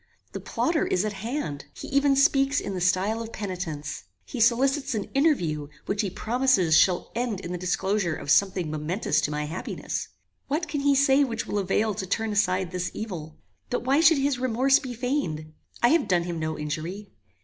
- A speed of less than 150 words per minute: No, average, 195 wpm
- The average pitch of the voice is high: Yes, high, 210 Hz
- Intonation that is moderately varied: No, wide, 7.1 semitones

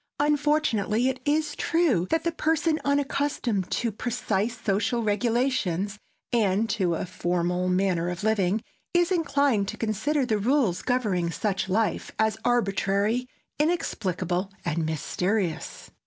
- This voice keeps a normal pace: No, slow, 125 wpm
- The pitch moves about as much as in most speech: No, wide, 6.5 semitones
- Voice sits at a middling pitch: No, high, 220 Hz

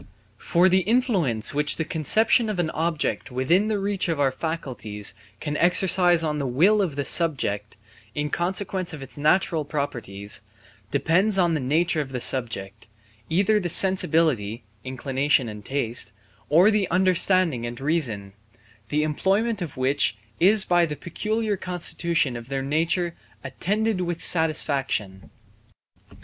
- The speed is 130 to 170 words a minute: Yes, average, 140 wpm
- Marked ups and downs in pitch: Yes, wide, 5.7 semitones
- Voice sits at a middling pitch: Yes, medium, 160 Hz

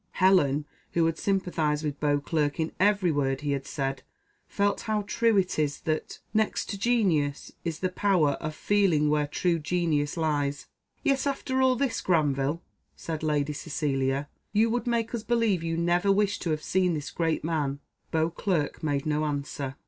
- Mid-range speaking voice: Yes, medium, 160 Hz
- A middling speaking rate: Yes, average, 170 wpm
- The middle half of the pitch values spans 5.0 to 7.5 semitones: Yes, average, 5.3 semitones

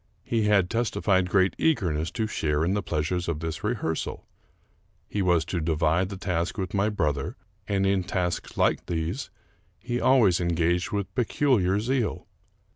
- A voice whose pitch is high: No, very low, 95 Hz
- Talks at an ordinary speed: Yes, average, 155 wpm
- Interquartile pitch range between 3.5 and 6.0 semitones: Yes, average, 3.8 semitones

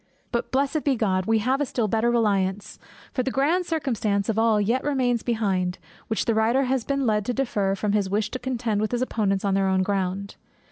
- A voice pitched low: No, high, 225 Hz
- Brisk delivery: Yes, fast, 220 wpm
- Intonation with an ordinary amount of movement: Yes, average, 4.2 semitones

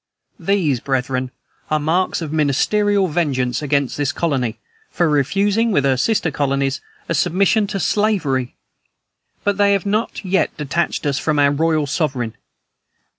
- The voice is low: No, medium, 155 Hz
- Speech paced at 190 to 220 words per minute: No, average, 140 wpm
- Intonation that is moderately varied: No, wide, 6.1 semitones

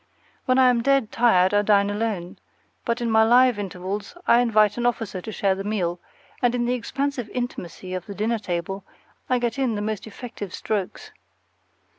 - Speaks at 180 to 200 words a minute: Yes, average, 185 wpm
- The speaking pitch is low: No, high, 220 Hz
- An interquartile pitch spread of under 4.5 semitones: Yes, average, 3.5 semitones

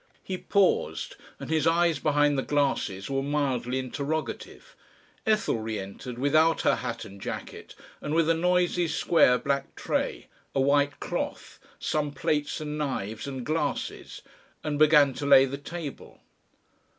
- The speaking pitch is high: No, medium, 145 Hz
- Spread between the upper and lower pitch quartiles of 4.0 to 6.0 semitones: No, average, 3.0 semitones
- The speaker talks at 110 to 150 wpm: Yes, average, 145 wpm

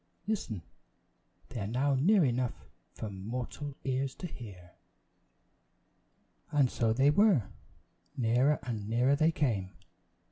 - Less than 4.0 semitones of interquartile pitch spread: No, average, 4.4 semitones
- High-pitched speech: No, low, 125 Hz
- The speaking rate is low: Yes, slow, 115 wpm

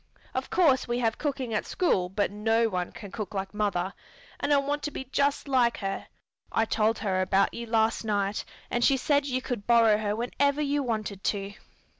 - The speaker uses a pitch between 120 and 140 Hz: No, high, 225 Hz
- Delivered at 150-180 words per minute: No, average, 200 wpm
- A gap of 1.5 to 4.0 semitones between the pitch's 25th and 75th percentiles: No, average, 4.5 semitones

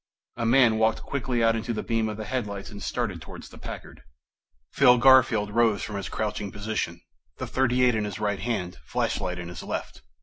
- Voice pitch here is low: Yes, low, 110 Hz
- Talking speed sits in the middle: Yes, average, 195 wpm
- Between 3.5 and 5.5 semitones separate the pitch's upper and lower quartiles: No, average, 2.9 semitones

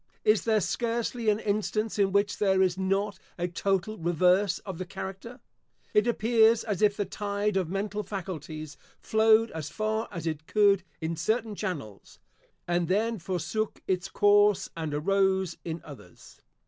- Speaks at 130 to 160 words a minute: Yes, average, 155 wpm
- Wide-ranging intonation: No, average, 3.4 semitones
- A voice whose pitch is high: Yes, high, 195 Hz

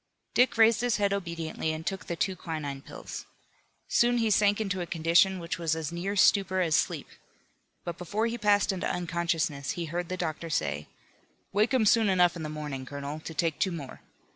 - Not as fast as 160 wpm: No, average, 195 wpm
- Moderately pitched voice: Yes, medium, 175 Hz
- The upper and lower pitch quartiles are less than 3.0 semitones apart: No, average, 4.0 semitones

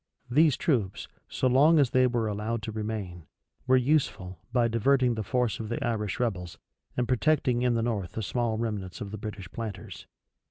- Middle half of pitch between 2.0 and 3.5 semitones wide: Yes, average, 3.1 semitones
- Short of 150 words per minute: No, average, 185 wpm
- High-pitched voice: No, low, 115 Hz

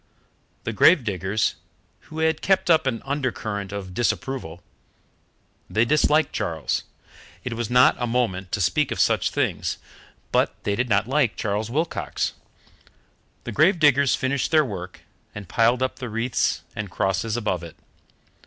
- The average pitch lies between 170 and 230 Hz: No, low, 115 Hz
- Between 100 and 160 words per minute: Yes, average, 150 wpm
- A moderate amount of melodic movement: No, wide, 5.7 semitones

